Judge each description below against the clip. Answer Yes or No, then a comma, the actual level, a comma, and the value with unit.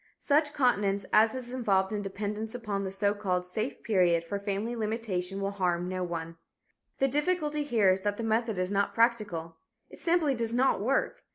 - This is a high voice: Yes, high, 210 Hz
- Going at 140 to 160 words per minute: No, average, 185 wpm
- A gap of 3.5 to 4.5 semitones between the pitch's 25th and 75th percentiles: Yes, average, 3.9 semitones